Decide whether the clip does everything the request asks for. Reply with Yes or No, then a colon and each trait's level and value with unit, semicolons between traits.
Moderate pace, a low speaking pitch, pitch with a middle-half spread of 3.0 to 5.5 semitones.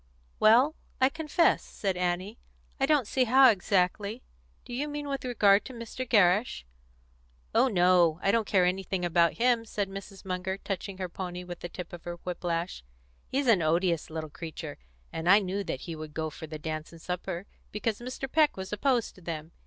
No: average, 190 wpm; high, 190 Hz; average, 5.0 semitones